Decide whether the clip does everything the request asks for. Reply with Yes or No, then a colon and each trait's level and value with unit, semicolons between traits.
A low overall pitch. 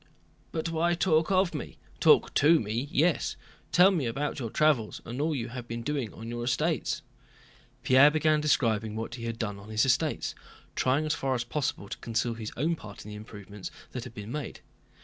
Yes: low, 125 Hz